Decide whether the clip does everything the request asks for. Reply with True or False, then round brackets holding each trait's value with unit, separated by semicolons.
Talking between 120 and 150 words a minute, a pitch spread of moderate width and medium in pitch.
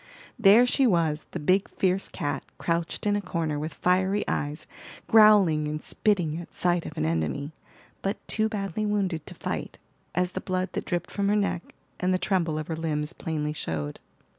False (185 wpm; 4.4 semitones; 175 Hz)